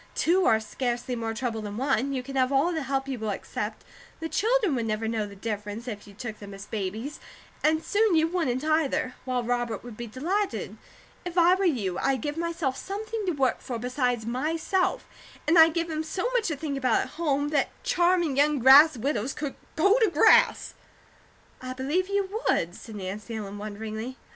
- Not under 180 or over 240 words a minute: Yes, average, 195 wpm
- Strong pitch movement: Yes, wide, 6.3 semitones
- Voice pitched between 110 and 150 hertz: No, very high, 270 Hz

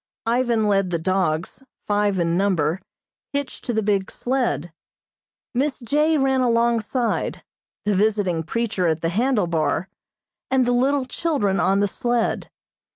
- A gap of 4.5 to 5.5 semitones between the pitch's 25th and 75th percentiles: Yes, average, 4.9 semitones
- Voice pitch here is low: No, high, 210 Hz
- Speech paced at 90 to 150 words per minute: Yes, average, 140 wpm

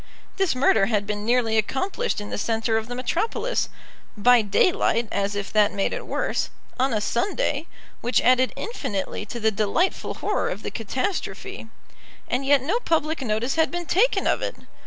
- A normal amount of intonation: No, wide, 7.1 semitones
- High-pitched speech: Yes, high, 245 Hz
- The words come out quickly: No, average, 175 wpm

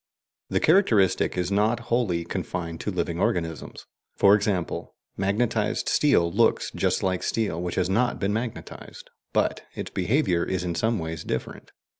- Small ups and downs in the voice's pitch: No, average, 4.4 semitones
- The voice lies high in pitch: No, very low, 95 Hz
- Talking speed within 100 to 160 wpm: Yes, average, 150 wpm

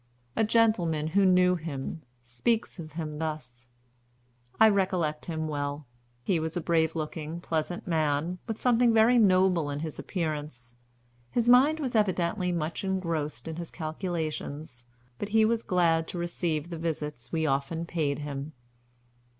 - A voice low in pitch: No, medium, 165 Hz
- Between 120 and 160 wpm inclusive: Yes, average, 150 wpm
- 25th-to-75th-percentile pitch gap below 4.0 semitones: Yes, average, 3.5 semitones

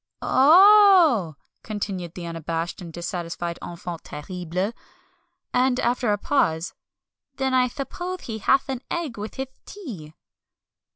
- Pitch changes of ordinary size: No, wide, 7.7 semitones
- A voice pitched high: Yes, high, 215 Hz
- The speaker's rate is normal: No, slow, 130 wpm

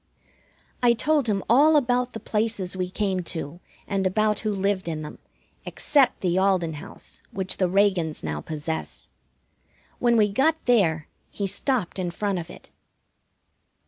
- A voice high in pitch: Yes, high, 195 Hz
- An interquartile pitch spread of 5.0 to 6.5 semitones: No, average, 4.5 semitones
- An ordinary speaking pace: Yes, average, 150 wpm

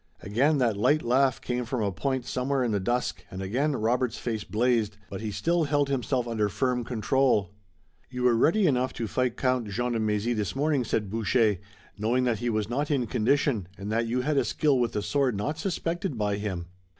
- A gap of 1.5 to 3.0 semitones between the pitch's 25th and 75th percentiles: No, average, 3.8 semitones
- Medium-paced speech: No, fast, 210 wpm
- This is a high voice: No, low, 120 Hz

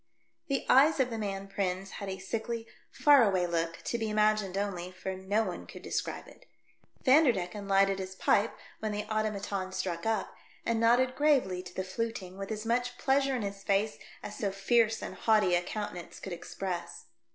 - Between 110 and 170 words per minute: No, average, 185 wpm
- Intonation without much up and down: No, average, 3.3 semitones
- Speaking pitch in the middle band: No, high, 205 Hz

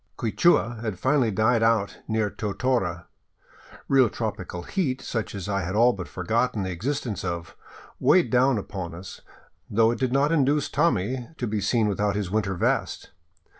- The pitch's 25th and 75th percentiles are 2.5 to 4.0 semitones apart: No, average, 4.4 semitones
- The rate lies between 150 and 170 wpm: Yes, average, 165 wpm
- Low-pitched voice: Yes, low, 110 Hz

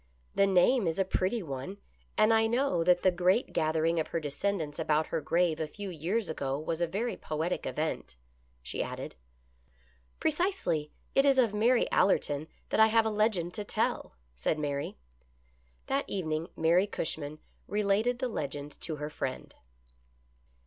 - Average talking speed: Yes, average, 165 wpm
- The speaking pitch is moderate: Yes, medium, 175 Hz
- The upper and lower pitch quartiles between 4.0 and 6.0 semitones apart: Yes, wide, 5.6 semitones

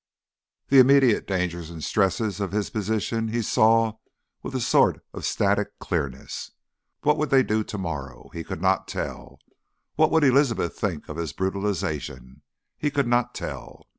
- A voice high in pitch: No, low, 105 Hz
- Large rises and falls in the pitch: Yes, wide, 6.2 semitones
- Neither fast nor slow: Yes, average, 160 wpm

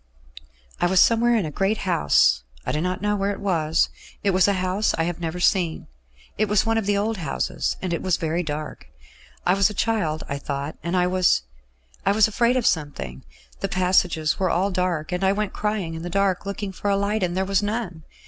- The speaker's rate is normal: No, fast, 225 wpm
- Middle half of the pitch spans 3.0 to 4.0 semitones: Yes, average, 3.3 semitones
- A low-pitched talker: No, medium, 185 Hz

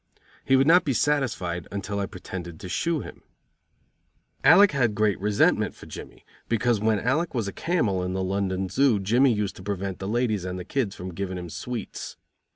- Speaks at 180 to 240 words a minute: Yes, average, 190 wpm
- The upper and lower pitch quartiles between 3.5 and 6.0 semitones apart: Yes, average, 5.2 semitones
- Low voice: Yes, low, 105 Hz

